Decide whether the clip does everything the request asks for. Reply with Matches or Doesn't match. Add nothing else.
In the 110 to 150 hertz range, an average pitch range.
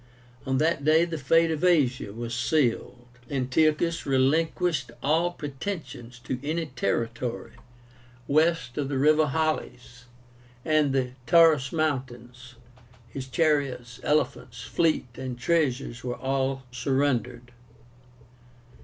Matches